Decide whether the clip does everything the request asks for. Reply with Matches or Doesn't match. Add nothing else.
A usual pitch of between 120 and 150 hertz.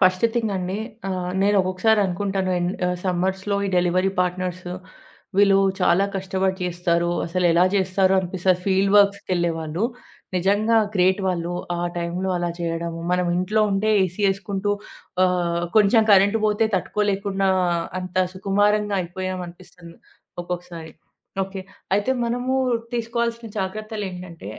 Doesn't match